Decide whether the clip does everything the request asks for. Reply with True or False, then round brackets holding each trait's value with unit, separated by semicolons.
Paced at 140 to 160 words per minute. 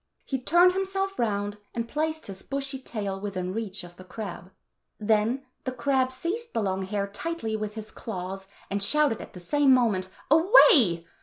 False (175 wpm)